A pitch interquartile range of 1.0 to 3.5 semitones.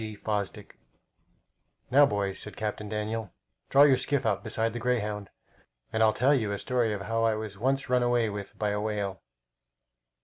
Yes: average, 2.8 semitones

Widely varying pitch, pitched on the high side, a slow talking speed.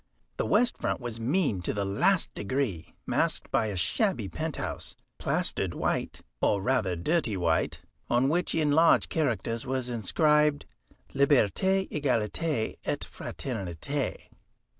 No: wide, 6.7 semitones; low, 130 Hz; slow, 125 wpm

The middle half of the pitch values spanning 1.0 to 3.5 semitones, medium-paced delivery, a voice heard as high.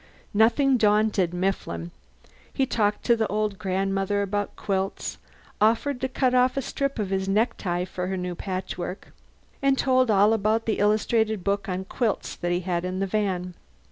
Yes: average, 3.1 semitones; average, 170 wpm; high, 205 Hz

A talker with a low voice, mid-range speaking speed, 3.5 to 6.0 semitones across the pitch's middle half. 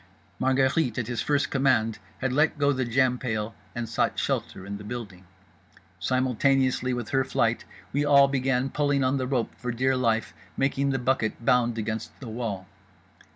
No: low, 125 Hz; average, 170 wpm; average, 2.8 semitones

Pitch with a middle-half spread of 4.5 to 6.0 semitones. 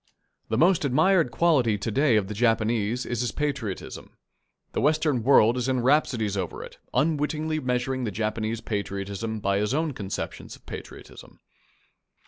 Yes: wide, 5.4 semitones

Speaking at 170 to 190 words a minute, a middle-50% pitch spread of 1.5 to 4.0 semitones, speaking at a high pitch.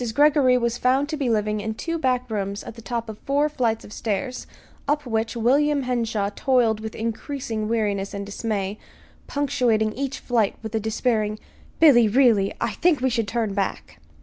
Yes: average, 175 wpm; average, 3.5 semitones; high, 230 Hz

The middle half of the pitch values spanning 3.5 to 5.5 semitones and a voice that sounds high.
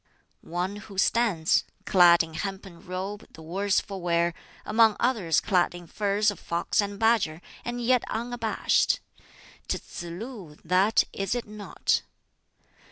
Yes: average, 4.0 semitones; high, 195 Hz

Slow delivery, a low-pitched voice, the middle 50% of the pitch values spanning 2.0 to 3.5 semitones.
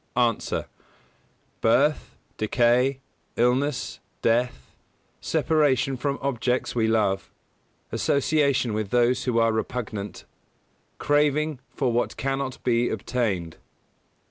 Yes: slow, 95 wpm; low, 125 Hz; average, 3.1 semitones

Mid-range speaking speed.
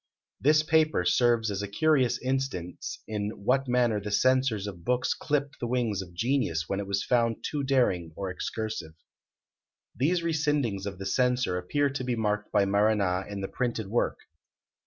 Yes: average, 170 wpm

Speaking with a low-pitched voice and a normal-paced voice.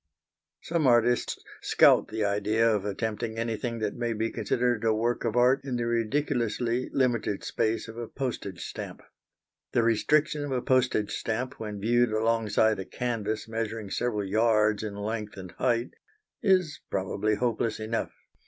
Yes: low, 115 Hz; average, 155 wpm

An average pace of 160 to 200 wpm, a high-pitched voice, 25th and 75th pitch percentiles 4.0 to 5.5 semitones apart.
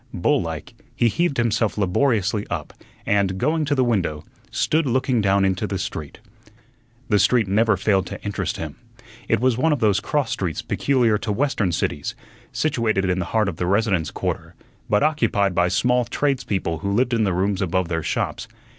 No: average, 180 wpm; low, 105 Hz; average, 4.7 semitones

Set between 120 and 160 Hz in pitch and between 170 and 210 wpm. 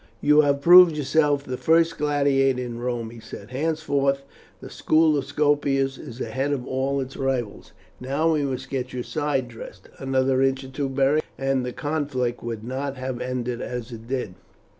Yes: low, 135 Hz; average, 180 wpm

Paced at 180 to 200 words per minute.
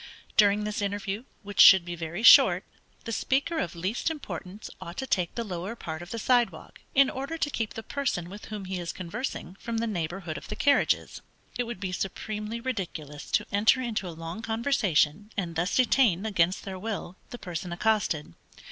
Yes: average, 190 wpm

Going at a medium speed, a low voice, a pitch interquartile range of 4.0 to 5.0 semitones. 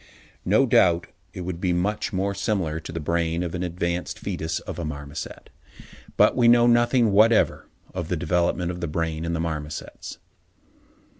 No: average, 170 wpm; very low, 85 Hz; average, 3.0 semitones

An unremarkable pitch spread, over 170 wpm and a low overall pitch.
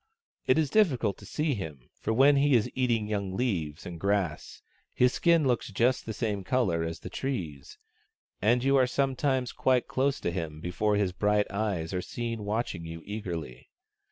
No: wide, 6.3 semitones; average, 180 wpm; low, 105 Hz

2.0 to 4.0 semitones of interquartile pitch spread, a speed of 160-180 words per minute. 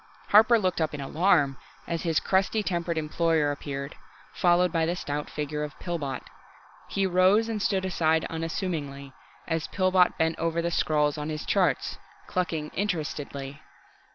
No: average, 3.5 semitones; average, 150 wpm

